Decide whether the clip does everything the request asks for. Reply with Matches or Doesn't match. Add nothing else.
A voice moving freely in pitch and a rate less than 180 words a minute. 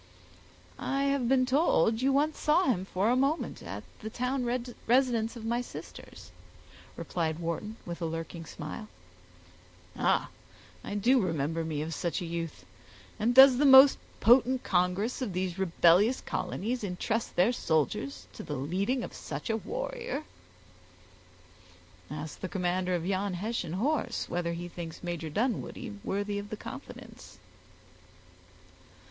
Matches